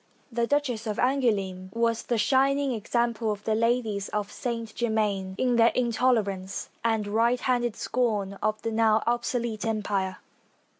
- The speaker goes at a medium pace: Yes, average, 145 wpm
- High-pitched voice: Yes, high, 225 Hz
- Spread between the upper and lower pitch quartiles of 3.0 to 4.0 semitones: No, narrow, 2.4 semitones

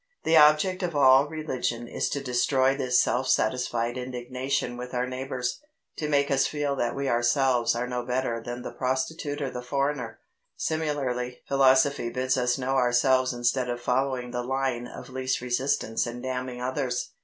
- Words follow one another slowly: No, average, 165 wpm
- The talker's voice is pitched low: Yes, low, 130 Hz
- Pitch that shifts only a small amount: Yes, narrow, 2.0 semitones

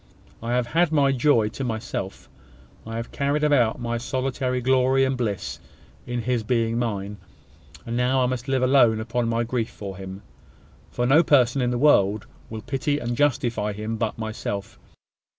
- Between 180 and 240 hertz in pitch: No, low, 120 Hz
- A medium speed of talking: Yes, average, 175 wpm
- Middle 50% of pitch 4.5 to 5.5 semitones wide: No, average, 2.9 semitones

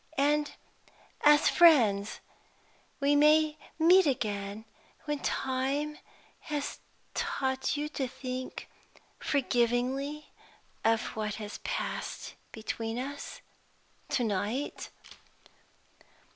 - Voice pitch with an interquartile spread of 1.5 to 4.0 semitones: No, average, 4.6 semitones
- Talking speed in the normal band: No, slow, 85 wpm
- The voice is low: No, very high, 265 Hz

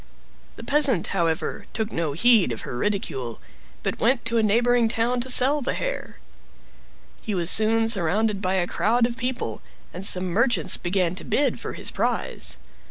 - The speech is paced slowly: No, average, 170 wpm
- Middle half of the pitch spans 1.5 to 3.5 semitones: No, average, 4.9 semitones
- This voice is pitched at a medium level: No, high, 220 Hz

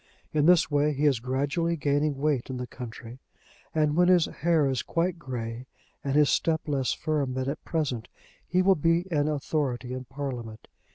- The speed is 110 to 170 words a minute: No, average, 180 wpm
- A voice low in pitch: No, medium, 145 Hz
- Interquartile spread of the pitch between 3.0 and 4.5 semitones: Yes, average, 3.5 semitones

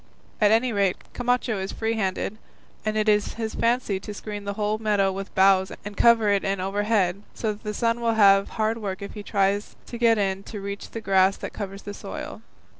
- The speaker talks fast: Yes, fast, 215 wpm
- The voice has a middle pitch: No, high, 205 Hz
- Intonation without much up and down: Yes, narrow, 2.1 semitones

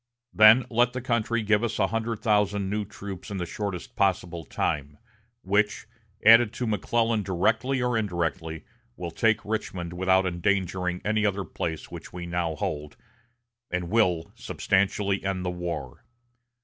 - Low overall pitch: Yes, low, 100 Hz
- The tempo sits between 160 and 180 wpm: No, average, 150 wpm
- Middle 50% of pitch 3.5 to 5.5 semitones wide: Yes, average, 3.9 semitones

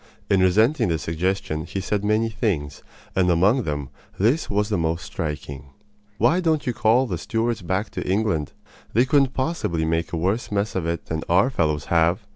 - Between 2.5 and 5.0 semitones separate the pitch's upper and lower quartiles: No, wide, 5.5 semitones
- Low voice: Yes, very low, 95 Hz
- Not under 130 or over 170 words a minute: No, average, 185 wpm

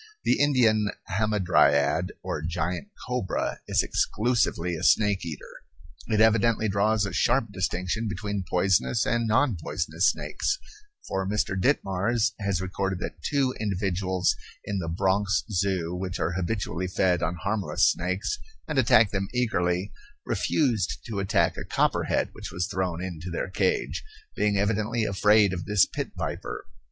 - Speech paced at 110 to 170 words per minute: Yes, average, 145 wpm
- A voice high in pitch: No, very low, 95 Hz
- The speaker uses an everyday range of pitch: Yes, average, 3.3 semitones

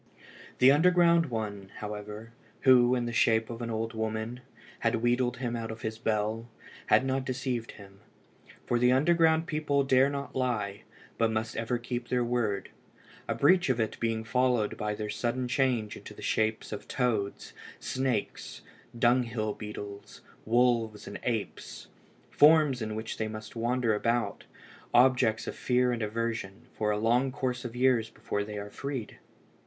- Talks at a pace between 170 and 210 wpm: No, average, 160 wpm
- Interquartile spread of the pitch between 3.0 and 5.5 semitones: No, narrow, 2.6 semitones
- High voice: No, low, 120 Hz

